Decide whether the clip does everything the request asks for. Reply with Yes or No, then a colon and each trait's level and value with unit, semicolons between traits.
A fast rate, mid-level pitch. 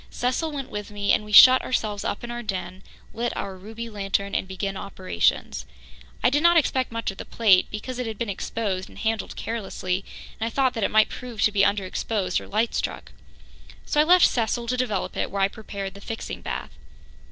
No: fast, 210 wpm; high, 215 Hz